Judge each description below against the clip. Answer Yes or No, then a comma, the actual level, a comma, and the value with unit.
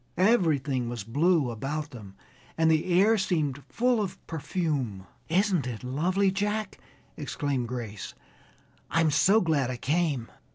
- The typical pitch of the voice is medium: Yes, medium, 155 Hz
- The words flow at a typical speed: No, slow, 130 wpm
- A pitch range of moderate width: No, wide, 6.4 semitones